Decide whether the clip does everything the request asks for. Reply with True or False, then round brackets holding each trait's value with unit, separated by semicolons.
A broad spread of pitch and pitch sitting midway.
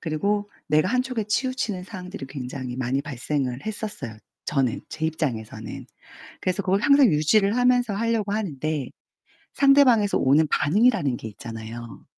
True (8.3 semitones; 180 Hz)